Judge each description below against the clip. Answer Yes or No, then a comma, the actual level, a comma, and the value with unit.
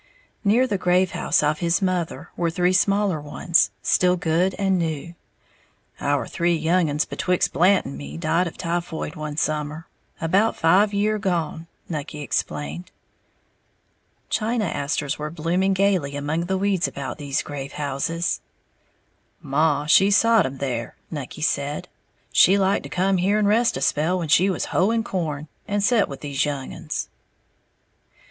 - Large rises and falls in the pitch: No, average, 4.4 semitones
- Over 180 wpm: No, average, 155 wpm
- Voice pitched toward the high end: No, medium, 170 Hz